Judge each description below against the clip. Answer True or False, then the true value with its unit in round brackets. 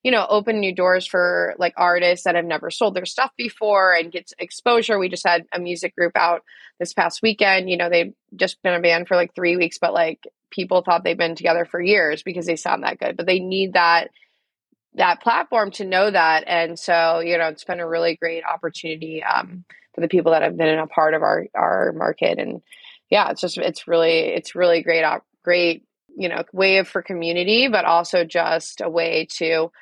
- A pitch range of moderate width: False (2.1 semitones)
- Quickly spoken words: True (215 wpm)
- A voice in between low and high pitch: True (175 Hz)